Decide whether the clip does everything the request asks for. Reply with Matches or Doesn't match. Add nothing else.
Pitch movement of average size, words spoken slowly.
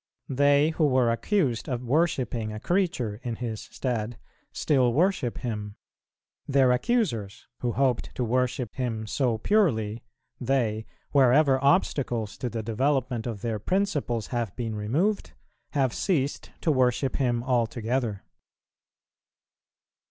Matches